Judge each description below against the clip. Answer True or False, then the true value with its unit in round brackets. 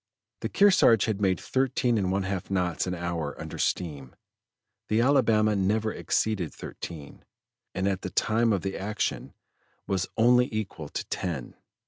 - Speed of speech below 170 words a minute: True (150 wpm)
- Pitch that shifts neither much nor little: True (3.6 semitones)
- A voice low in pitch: True (100 Hz)